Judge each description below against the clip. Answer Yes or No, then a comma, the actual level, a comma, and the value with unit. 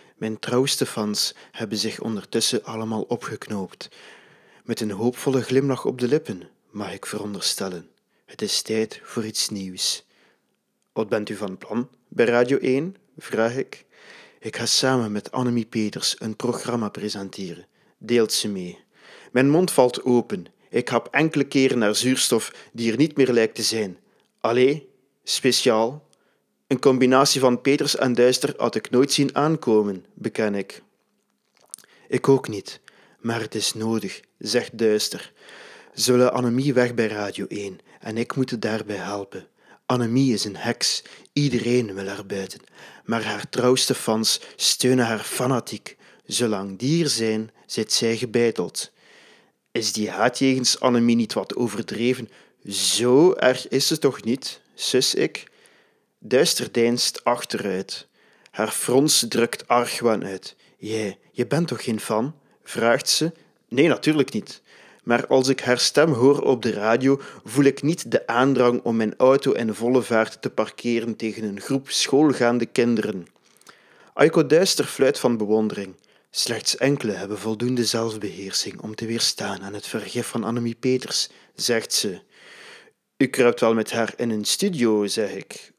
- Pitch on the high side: No, low, 120 Hz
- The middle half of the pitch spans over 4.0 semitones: No, average, 3.2 semitones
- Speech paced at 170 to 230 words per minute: No, average, 150 wpm